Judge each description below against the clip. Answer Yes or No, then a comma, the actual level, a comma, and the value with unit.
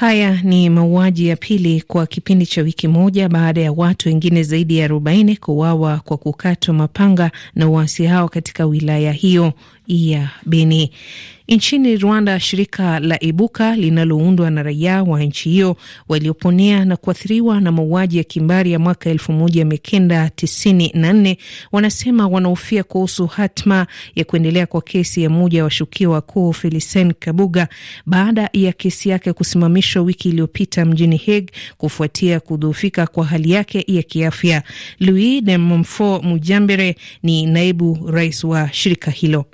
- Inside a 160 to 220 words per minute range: No, average, 135 wpm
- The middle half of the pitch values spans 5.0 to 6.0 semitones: No, average, 2.8 semitones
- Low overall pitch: No, medium, 170 Hz